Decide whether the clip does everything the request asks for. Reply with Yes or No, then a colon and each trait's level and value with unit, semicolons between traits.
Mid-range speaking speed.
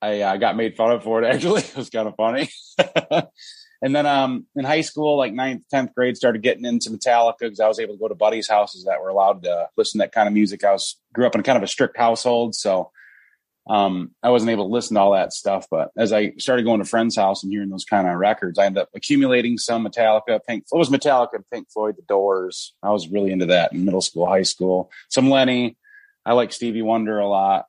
No: fast, 245 wpm